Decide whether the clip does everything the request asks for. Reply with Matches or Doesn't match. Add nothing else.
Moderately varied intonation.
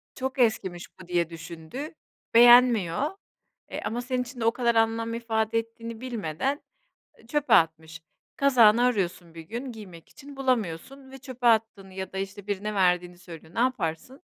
Doesn't match